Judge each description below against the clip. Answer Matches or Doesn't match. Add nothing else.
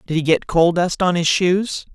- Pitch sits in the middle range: Matches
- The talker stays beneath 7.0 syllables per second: Matches